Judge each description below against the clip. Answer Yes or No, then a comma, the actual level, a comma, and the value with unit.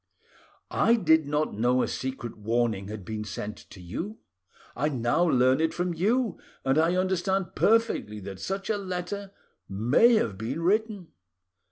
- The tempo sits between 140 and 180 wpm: Yes, average, 155 wpm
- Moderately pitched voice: Yes, medium, 160 Hz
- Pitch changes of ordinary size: No, wide, 9.0 semitones